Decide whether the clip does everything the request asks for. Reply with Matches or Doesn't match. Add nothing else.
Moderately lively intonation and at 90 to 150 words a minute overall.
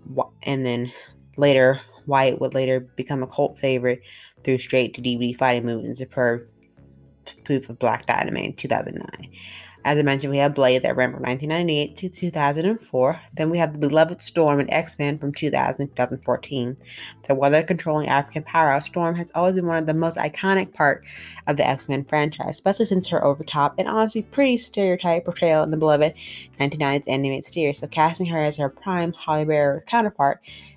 Doesn't match